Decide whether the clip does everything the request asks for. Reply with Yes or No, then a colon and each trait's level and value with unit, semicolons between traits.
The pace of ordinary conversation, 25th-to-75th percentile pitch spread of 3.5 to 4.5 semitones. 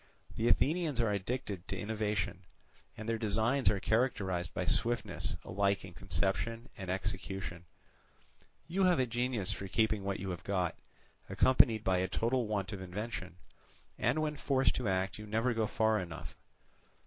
Yes: average, 160 wpm; average, 3.8 semitones